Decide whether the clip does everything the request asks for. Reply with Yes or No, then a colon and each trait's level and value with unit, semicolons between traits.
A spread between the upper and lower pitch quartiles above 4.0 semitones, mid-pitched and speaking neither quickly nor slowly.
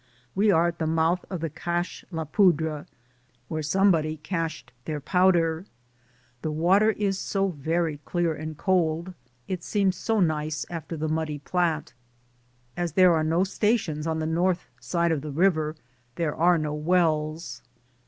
No: narrow, 2.6 semitones; medium, 165 Hz; average, 160 wpm